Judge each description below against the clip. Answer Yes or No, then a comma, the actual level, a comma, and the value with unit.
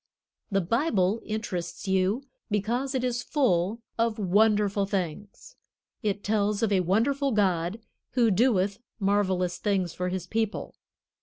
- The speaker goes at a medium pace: No, slow, 130 wpm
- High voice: Yes, high, 205 Hz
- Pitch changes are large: No, average, 3.4 semitones